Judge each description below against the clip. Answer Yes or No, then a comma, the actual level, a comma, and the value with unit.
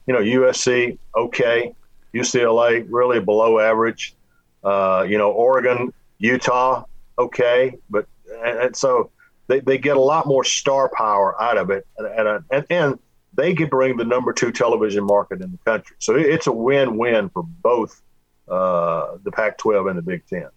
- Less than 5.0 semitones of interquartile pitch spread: Yes, average, 3.8 semitones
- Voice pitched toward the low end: Yes, low, 125 Hz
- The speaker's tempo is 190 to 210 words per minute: No, average, 170 wpm